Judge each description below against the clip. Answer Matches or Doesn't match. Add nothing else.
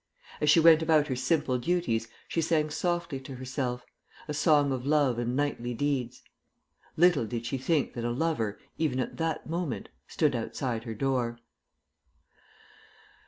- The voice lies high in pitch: Doesn't match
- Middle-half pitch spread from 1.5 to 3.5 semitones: Doesn't match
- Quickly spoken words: Doesn't match